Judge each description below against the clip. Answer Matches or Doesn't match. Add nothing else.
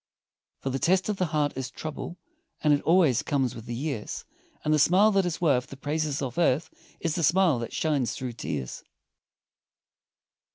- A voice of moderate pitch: Matches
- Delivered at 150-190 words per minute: Matches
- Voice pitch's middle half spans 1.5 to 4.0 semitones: Doesn't match